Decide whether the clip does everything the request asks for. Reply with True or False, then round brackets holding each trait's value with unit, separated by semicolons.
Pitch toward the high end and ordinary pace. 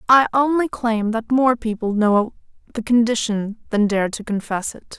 True (225 Hz; 170 wpm)